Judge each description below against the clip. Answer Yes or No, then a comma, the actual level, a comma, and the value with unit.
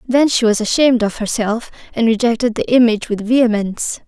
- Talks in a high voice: Yes, high, 230 Hz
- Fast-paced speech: No, average, 175 wpm